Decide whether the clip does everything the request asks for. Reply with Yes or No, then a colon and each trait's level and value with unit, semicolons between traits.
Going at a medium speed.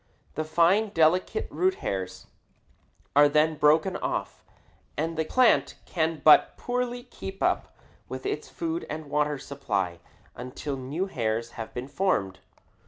No: slow, 130 wpm